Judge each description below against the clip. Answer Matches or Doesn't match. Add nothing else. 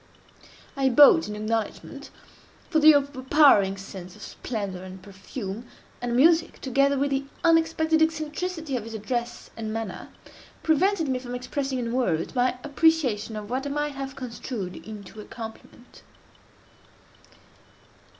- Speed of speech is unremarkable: Doesn't match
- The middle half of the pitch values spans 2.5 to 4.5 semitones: Doesn't match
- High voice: Matches